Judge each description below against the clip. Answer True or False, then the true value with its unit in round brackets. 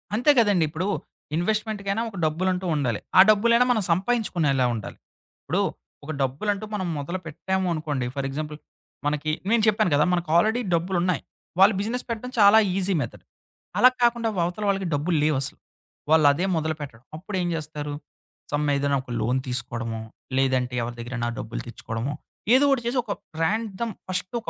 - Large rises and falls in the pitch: True (6.6 semitones)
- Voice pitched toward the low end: False (170 Hz)